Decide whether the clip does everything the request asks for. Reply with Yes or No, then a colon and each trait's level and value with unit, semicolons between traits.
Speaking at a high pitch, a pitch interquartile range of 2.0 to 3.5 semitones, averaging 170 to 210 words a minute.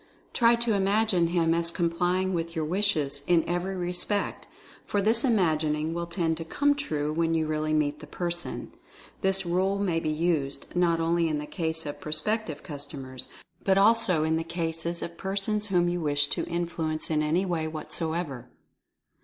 No: medium, 170 Hz; average, 3.2 semitones; average, 180 wpm